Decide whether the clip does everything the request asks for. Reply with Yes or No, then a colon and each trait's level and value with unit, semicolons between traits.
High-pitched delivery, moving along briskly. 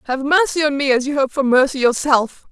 Yes: very high, 275 Hz; fast, 240 wpm